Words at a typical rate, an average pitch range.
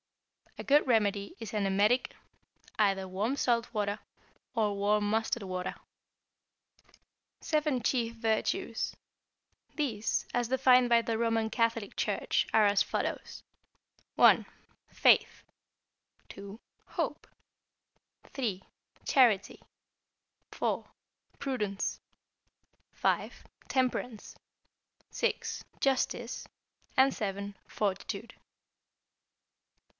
No: slow, 85 wpm; average, 3.3 semitones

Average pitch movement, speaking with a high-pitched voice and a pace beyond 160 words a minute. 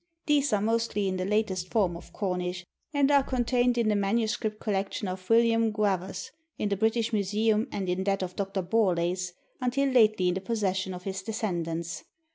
Yes: average, 3.5 semitones; high, 205 Hz; average, 180 wpm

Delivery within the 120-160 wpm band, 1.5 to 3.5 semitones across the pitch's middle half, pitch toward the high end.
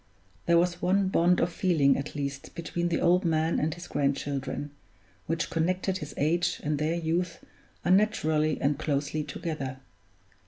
No: average, 150 wpm; average, 3.0 semitones; medium, 160 Hz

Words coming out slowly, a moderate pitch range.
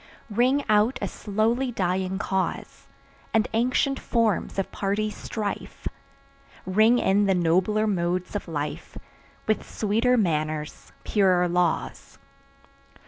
Yes: slow, 110 wpm; average, 3.5 semitones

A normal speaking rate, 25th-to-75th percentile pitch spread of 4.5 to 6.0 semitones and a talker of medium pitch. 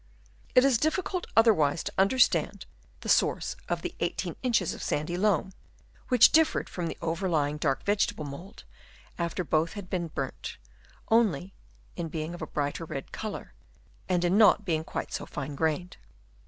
Yes: average, 160 wpm; average, 5.1 semitones; medium, 175 Hz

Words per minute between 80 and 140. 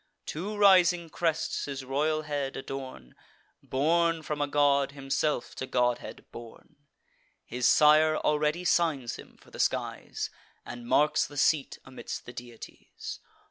Yes: slow, 135 wpm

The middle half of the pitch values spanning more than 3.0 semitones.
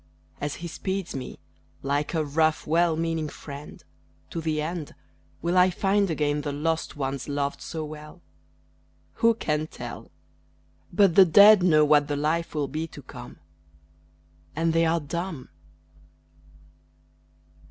No: narrow, 2.5 semitones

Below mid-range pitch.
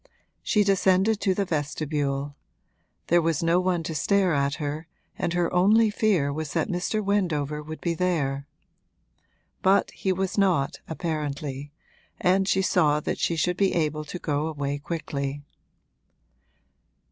No: medium, 165 Hz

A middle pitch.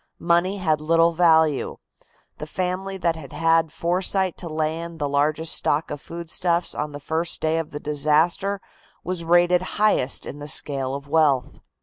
Yes: medium, 165 Hz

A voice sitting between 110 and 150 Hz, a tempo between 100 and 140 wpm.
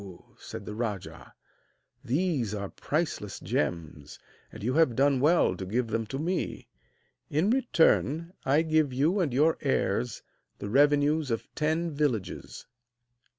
Yes: medium, 140 Hz; slow, 135 wpm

